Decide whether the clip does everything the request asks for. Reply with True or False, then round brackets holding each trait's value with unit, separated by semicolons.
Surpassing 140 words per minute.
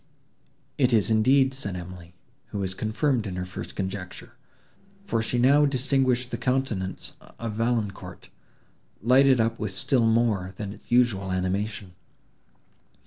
False (135 wpm)